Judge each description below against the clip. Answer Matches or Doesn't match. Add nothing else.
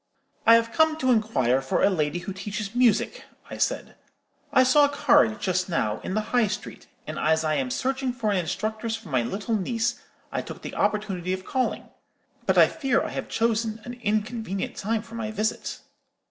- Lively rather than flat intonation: Doesn't match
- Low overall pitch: Doesn't match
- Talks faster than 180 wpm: Matches